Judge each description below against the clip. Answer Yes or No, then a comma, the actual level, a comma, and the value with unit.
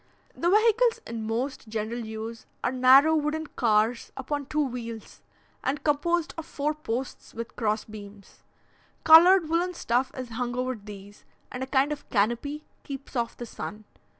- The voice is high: Yes, very high, 255 Hz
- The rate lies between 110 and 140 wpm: No, average, 155 wpm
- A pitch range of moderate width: Yes, average, 5.0 semitones